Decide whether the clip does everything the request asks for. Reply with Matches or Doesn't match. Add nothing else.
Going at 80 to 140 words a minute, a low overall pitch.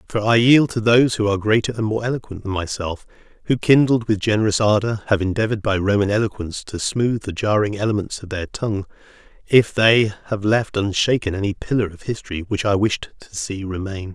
Doesn't match